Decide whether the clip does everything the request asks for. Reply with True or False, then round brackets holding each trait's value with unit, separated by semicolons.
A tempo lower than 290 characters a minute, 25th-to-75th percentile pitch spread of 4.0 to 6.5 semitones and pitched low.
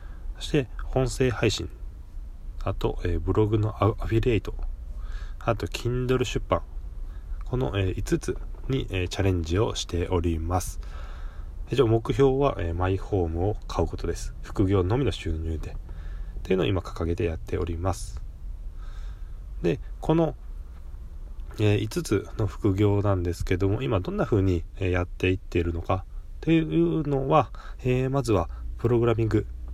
True (265 characters per minute; 5.5 semitones; 90 Hz)